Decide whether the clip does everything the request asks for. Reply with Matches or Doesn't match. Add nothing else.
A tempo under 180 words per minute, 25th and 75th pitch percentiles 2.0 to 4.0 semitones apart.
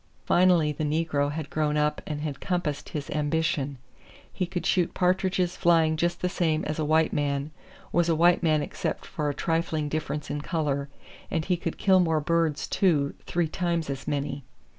Doesn't match